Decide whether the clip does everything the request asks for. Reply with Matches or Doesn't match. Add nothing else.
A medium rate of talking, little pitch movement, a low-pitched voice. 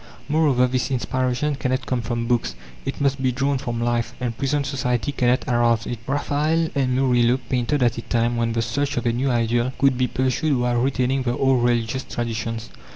Matches